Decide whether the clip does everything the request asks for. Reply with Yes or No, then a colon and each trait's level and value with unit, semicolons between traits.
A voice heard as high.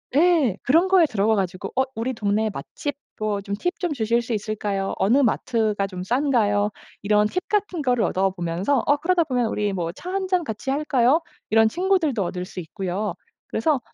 Yes: high, 225 Hz